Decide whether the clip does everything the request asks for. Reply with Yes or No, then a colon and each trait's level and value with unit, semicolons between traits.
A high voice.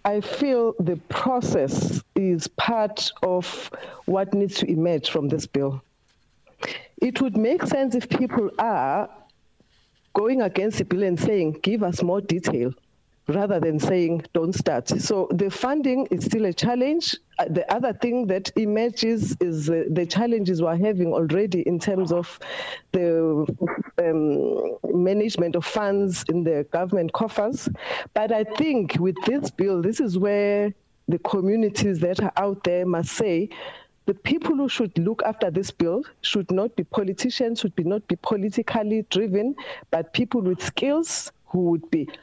Yes: high, 195 Hz